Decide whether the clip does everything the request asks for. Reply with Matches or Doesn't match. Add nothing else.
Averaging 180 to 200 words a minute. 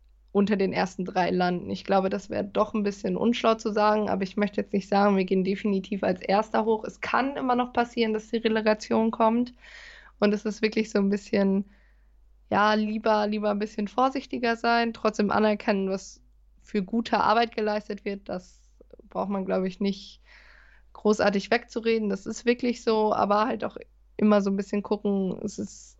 Matches